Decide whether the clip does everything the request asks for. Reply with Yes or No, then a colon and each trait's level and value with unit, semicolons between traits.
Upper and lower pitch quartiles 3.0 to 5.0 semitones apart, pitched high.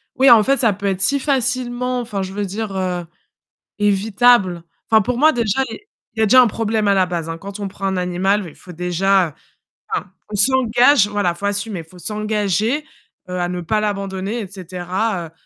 Yes: average, 3.6 semitones; high, 205 Hz